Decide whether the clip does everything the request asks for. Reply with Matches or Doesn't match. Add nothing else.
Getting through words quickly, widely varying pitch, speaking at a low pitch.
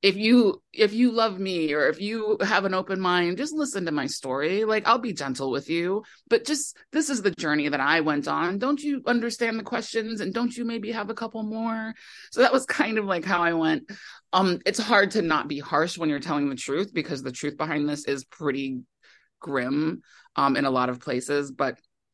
Doesn't match